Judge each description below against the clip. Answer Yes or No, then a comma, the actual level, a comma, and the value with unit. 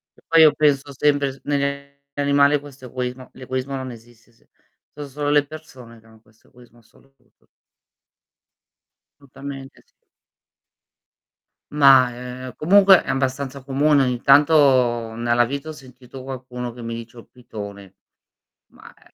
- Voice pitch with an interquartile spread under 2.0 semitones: No, average, 2.7 semitones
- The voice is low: Yes, low, 130 Hz